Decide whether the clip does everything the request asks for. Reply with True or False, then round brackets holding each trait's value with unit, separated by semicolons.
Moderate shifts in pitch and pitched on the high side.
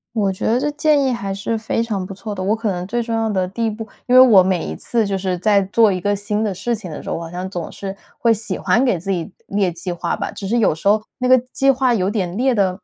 True (3.6 semitones; 205 Hz)